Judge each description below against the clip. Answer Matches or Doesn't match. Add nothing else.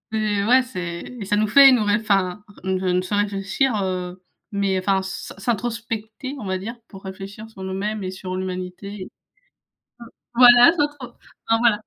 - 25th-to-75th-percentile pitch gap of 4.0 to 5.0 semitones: Doesn't match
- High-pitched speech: Matches